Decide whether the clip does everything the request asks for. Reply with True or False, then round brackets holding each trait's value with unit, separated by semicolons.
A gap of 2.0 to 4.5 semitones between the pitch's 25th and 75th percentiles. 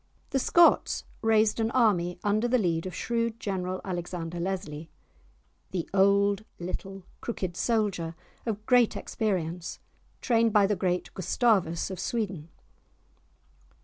True (4.0 semitones)